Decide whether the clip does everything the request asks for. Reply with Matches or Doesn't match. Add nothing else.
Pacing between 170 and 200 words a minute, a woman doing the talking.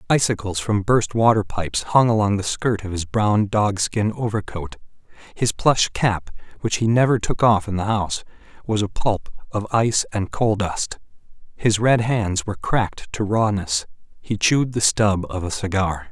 Doesn't match